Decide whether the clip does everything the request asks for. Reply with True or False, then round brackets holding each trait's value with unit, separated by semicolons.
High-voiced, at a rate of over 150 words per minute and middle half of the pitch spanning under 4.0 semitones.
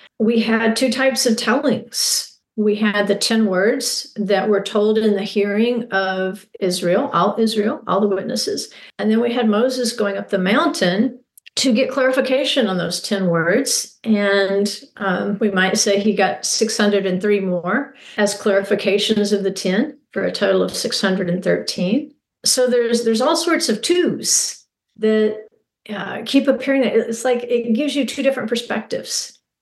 True (220 Hz; 160 wpm; 3.6 semitones)